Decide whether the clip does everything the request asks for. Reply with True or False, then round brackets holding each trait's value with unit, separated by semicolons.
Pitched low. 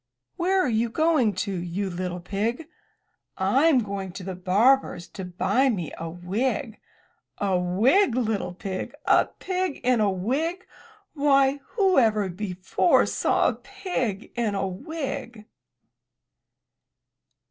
False (215 Hz)